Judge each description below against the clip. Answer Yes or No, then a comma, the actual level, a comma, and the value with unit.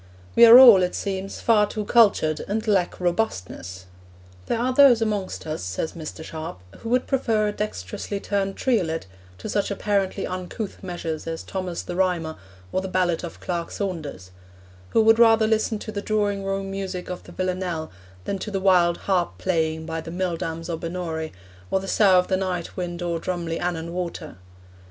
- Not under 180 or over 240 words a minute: Yes, average, 185 wpm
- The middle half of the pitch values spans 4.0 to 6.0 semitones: No, average, 3.6 semitones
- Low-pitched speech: No, medium, 185 Hz